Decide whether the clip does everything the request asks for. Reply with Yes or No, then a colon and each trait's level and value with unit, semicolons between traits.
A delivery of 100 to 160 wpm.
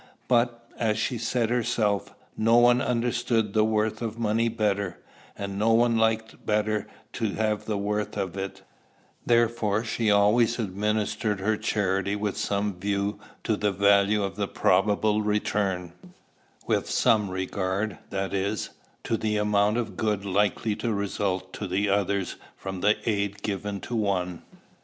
Yes: average, 145 wpm